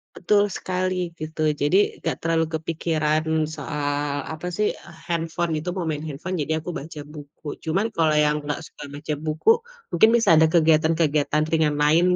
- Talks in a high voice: No, medium, 160 Hz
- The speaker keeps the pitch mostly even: Yes, narrow, 2.2 semitones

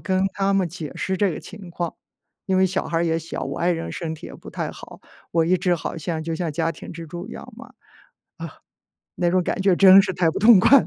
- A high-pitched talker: No, medium, 180 Hz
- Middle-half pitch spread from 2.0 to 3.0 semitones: Yes, narrow, 2.4 semitones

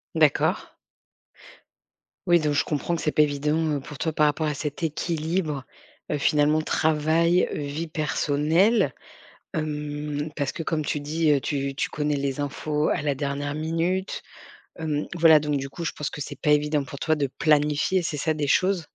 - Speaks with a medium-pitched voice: Yes, medium, 150 Hz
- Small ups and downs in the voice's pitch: Yes, narrow, 1.7 semitones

